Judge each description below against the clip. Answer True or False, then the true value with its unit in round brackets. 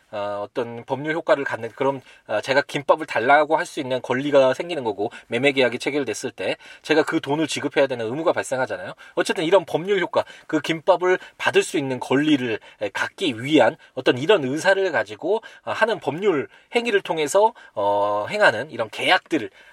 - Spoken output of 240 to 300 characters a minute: False (360 characters per minute)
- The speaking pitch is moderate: True (155 Hz)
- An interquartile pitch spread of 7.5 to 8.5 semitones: True (7.8 semitones)